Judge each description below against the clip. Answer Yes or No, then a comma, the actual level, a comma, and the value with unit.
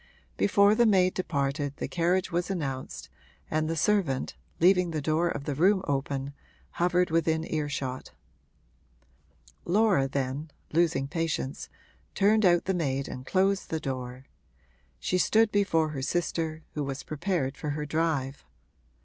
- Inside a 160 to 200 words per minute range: No, average, 140 wpm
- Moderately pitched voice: Yes, medium, 160 Hz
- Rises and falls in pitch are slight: No, average, 4.6 semitones